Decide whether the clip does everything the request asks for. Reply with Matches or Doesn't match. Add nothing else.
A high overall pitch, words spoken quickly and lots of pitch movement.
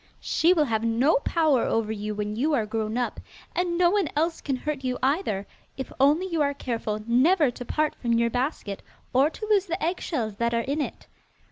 Matches